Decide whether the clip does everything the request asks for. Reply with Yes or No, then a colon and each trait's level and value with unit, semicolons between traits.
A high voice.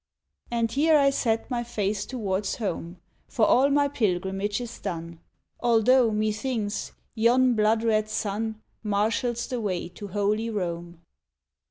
Yes: high, 215 Hz